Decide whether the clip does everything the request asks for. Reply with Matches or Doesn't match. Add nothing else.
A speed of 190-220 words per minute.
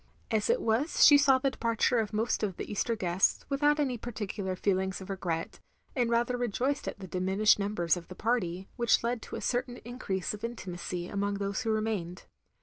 Matches